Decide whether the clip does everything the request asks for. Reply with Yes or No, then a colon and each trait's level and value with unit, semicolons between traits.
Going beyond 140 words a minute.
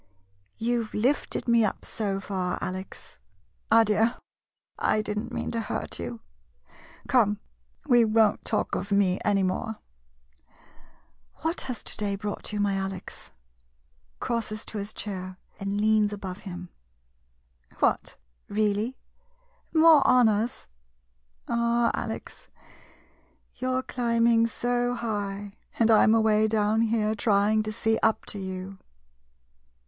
No: slow, 135 wpm